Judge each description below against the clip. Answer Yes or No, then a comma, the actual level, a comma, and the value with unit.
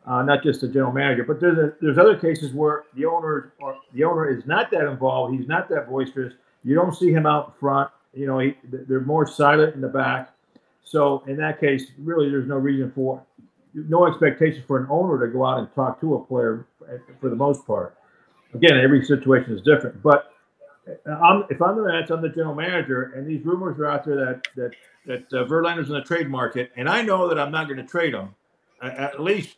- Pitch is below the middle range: No, medium, 145 Hz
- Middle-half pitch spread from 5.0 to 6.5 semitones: No, average, 3.3 semitones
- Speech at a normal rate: No, fast, 225 wpm